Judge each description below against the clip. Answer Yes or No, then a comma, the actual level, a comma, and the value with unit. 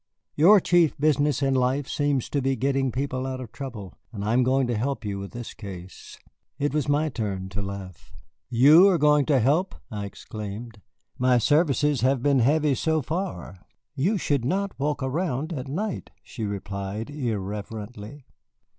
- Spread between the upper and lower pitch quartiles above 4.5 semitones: Yes, average, 5.2 semitones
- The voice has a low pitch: Yes, low, 130 Hz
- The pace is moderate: Yes, average, 170 wpm